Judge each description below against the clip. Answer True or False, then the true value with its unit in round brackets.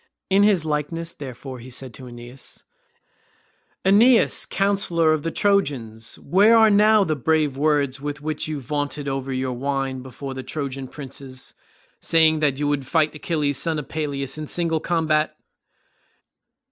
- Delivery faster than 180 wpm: False (150 wpm)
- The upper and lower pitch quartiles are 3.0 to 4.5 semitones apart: True (3.4 semitones)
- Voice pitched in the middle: True (150 Hz)